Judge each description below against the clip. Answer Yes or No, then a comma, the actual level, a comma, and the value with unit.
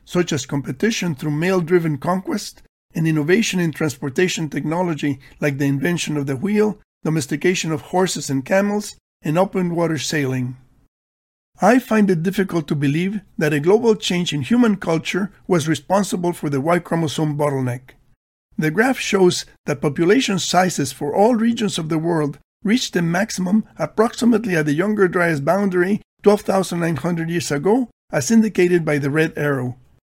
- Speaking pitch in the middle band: Yes, medium, 170 Hz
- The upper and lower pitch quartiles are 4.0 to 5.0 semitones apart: Yes, average, 4.5 semitones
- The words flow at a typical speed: Yes, average, 155 wpm